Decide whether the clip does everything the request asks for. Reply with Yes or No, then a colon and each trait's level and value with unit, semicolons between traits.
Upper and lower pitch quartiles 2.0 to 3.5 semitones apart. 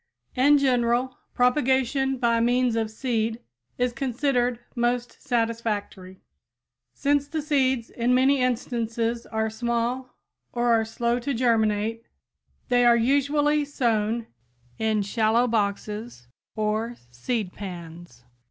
Yes: narrow, 2.5 semitones